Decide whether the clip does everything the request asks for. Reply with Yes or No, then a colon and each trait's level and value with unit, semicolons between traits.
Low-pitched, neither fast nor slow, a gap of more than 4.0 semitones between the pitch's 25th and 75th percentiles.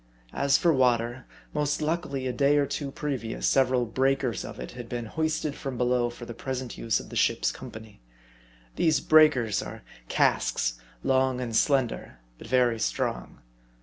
No: low, 130 Hz; average, 160 wpm; average, 3.0 semitones